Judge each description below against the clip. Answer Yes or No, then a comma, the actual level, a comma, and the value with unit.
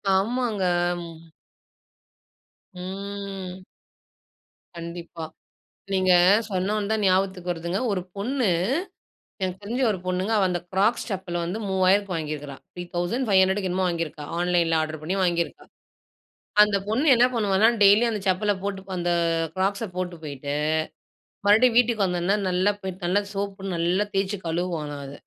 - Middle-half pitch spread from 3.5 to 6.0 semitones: No, narrow, 2.6 semitones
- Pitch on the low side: No, high, 190 Hz